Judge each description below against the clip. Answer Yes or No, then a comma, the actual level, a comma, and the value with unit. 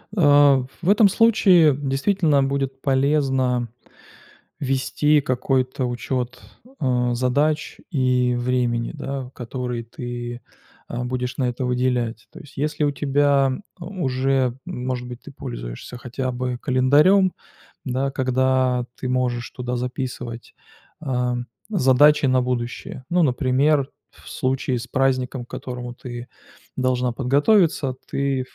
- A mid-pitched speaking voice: No, low, 130 Hz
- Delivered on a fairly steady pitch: Yes, narrow, 2.1 semitones